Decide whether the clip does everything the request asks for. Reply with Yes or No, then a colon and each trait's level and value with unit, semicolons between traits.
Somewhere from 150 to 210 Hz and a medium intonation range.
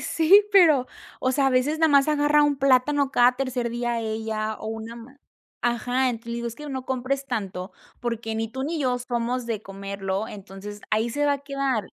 No: high, 245 Hz; average, 3.7 semitones